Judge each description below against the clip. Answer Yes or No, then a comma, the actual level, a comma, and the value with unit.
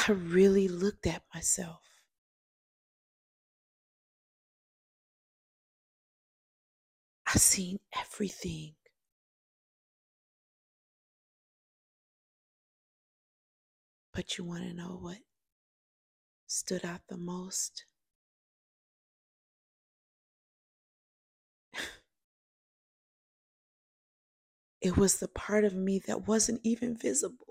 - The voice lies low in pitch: No, high, 195 Hz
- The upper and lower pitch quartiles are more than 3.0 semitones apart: No, average, 2.7 semitones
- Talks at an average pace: No, slow, 60 wpm